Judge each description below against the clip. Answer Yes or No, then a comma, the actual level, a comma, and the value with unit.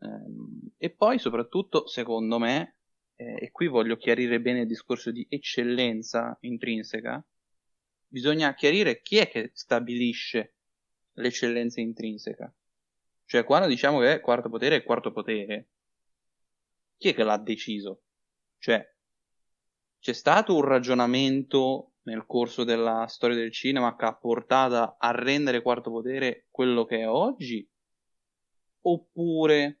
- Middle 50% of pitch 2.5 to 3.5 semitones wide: Yes, average, 2.8 semitones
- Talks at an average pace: Yes, average, 125 wpm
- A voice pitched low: Yes, low, 120 Hz